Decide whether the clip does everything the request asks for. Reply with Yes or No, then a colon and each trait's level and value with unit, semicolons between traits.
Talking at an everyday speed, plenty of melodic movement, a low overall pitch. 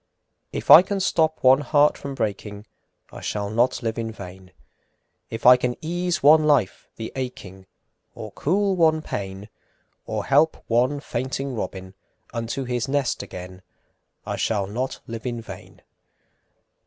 Yes: average, 150 wpm; wide, 5.7 semitones; low, 125 Hz